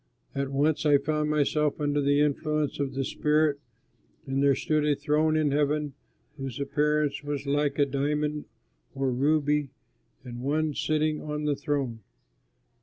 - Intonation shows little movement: Yes, narrow, 1.4 semitones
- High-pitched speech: No, medium, 145 Hz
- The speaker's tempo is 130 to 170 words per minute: Yes, average, 155 wpm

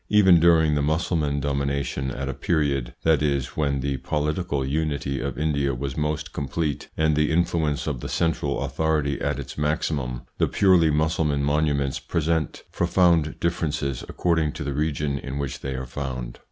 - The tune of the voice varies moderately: No, narrow, 2.3 semitones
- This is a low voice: Yes, very low, 75 Hz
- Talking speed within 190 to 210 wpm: No, average, 165 wpm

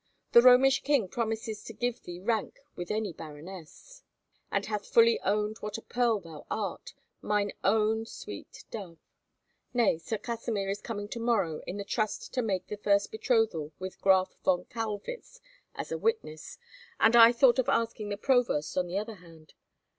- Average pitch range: Yes, average, 3.6 semitones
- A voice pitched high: Yes, high, 210 Hz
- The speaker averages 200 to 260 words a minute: No, average, 170 wpm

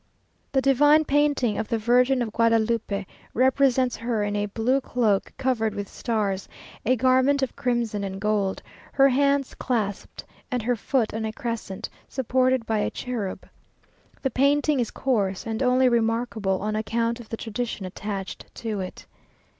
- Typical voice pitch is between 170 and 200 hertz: No, high, 230 Hz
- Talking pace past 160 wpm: No, average, 155 wpm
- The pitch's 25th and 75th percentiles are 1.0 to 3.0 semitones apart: No, average, 3.4 semitones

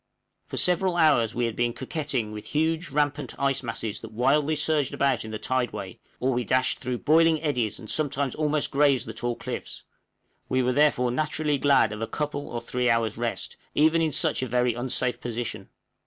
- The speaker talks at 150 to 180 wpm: No, average, 190 wpm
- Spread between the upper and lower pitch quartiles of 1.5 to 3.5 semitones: No, average, 3.9 semitones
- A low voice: Yes, low, 130 Hz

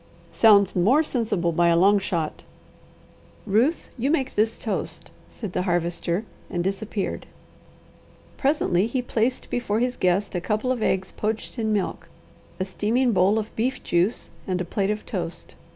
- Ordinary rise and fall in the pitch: Yes, average, 4.2 semitones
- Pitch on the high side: Yes, high, 210 Hz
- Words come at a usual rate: Yes, average, 155 wpm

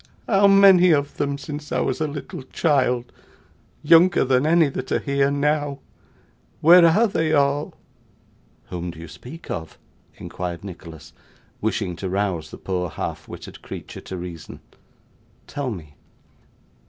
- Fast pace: No, average, 140 wpm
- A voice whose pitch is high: No, medium, 140 Hz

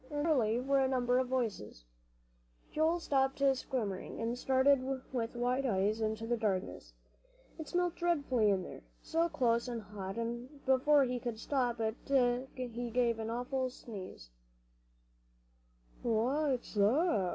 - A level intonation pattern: No, average, 3.3 semitones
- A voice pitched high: Yes, high, 245 Hz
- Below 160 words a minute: Yes, average, 140 wpm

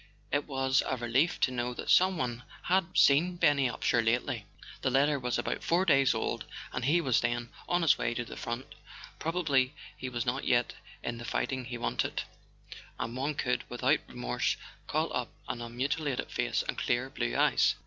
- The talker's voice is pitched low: Yes, low, 130 Hz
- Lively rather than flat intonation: No, average, 3.4 semitones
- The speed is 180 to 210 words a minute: Yes, average, 185 wpm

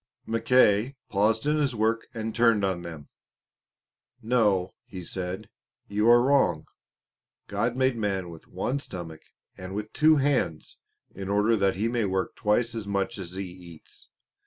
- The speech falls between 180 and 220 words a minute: No, average, 155 wpm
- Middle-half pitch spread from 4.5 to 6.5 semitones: No, average, 4.0 semitones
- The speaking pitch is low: Yes, low, 105 Hz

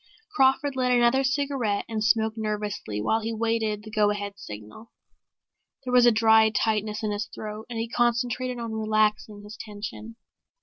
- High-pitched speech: Yes, high, 220 Hz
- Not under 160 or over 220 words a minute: Yes, average, 165 wpm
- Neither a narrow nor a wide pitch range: No, narrow, 2.1 semitones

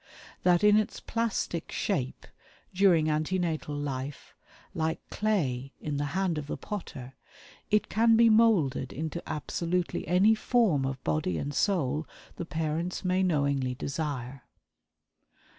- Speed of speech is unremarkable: No, slow, 130 wpm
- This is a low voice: No, medium, 160 Hz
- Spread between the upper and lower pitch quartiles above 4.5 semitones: Yes, wide, 5.4 semitones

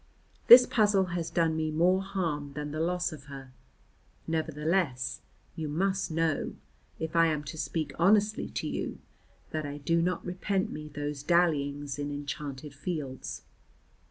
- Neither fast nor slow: Yes, average, 150 wpm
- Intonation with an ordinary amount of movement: Yes, average, 3.5 semitones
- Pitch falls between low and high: Yes, medium, 160 Hz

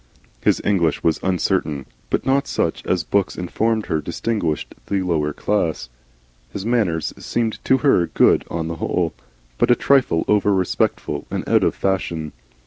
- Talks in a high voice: No, very low, 95 Hz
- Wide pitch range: No, average, 5.0 semitones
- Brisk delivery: No, average, 155 wpm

